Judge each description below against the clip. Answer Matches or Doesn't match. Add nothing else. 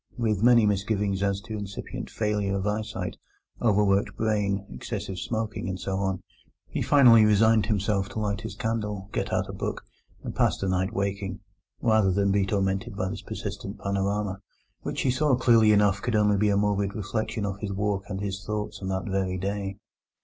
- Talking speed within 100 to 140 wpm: Doesn't match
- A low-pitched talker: Matches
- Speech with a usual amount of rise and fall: Doesn't match